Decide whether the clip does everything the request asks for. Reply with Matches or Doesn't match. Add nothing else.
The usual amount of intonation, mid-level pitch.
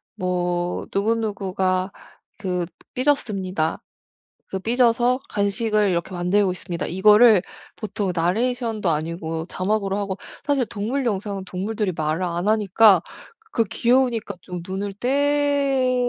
Doesn't match